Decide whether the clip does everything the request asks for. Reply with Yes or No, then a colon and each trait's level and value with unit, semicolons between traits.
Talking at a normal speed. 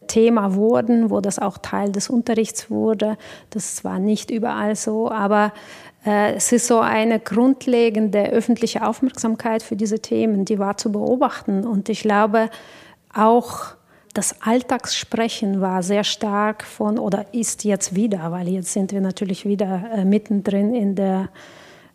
Yes: average, 150 wpm